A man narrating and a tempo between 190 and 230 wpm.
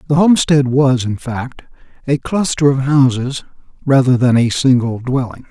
No: male; average, 155 wpm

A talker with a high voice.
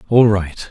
No: low, 105 Hz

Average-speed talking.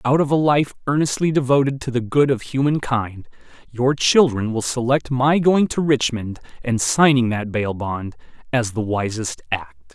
Yes: average, 175 wpm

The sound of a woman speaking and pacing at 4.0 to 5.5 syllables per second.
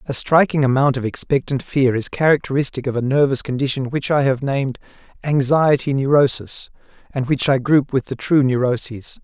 No: male; 5.3 syllables/s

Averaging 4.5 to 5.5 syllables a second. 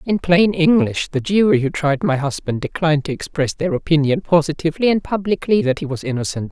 No: 5.7 syllables/s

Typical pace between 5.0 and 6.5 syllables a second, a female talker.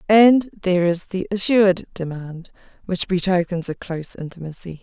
Yes: 5.1 syllables/s; female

